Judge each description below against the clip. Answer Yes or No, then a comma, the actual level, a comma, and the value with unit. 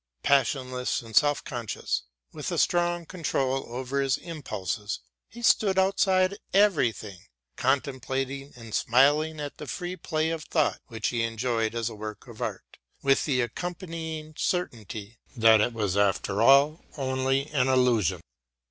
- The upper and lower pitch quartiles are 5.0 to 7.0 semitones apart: Yes, wide, 5.4 semitones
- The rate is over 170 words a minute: No, average, 140 wpm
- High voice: No, low, 135 Hz